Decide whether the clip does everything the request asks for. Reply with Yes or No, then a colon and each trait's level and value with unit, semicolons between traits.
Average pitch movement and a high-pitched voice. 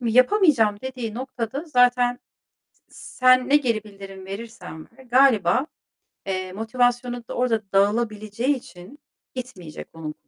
Yes: average, 3.7 semitones; high, 235 Hz